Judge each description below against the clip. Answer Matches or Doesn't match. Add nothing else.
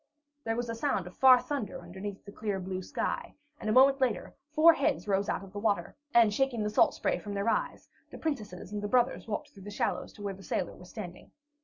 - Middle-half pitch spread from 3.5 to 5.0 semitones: Matches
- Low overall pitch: Doesn't match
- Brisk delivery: Matches